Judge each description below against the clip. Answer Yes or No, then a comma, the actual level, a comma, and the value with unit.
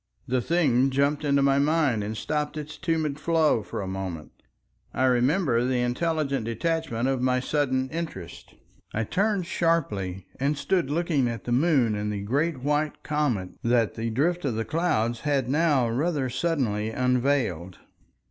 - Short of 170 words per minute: Yes, average, 155 wpm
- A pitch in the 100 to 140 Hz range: Yes, low, 135 Hz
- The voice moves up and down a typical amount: Yes, average, 4.8 semitones